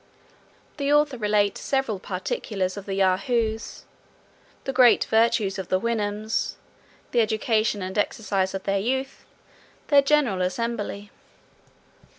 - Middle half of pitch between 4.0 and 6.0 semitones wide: No, average, 3.3 semitones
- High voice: Yes, high, 215 Hz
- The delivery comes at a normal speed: No, slow, 120 wpm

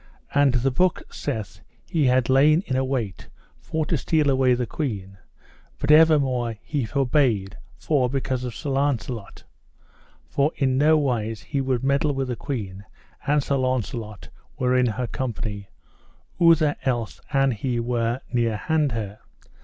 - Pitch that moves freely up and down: No, average, 3.4 semitones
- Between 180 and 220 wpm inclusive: No, average, 150 wpm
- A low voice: Yes, low, 130 Hz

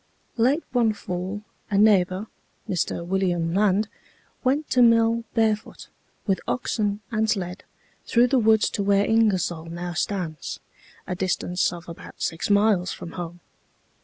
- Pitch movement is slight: No, average, 3.8 semitones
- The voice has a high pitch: Yes, high, 200 Hz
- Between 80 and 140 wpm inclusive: Yes, slow, 135 wpm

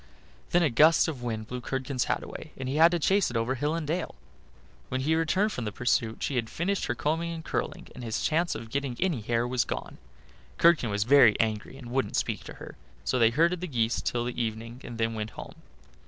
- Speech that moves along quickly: Yes, fast, 230 wpm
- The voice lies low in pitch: Yes, low, 130 Hz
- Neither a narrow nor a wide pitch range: No, wide, 5.8 semitones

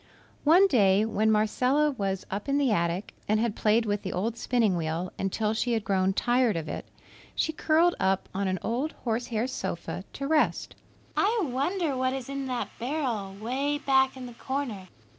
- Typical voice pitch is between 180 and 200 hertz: No, high, 235 Hz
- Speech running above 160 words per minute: Yes, average, 185 wpm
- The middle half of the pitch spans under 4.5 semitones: No, wide, 5.4 semitones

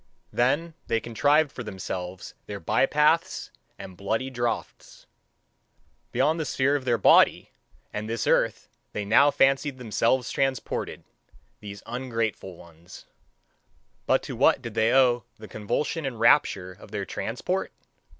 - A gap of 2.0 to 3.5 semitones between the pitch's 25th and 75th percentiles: No, average, 4.5 semitones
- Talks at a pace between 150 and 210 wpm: No, slow, 135 wpm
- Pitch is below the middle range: Yes, low, 120 Hz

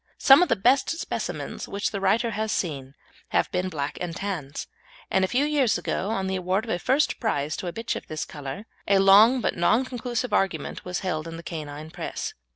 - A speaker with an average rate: No, fast, 215 wpm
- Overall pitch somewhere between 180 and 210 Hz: Yes, high, 190 Hz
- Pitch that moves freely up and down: Yes, wide, 5.7 semitones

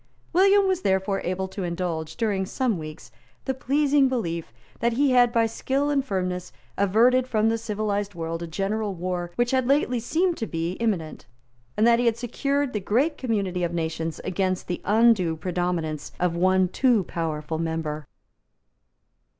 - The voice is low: No, high, 200 Hz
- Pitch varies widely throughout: Yes, wide, 6.0 semitones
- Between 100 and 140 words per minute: No, average, 165 wpm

